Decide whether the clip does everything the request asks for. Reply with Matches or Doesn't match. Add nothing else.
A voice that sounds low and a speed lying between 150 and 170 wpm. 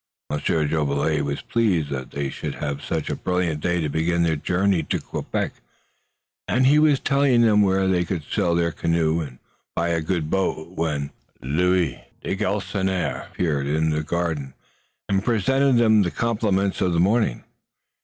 Matches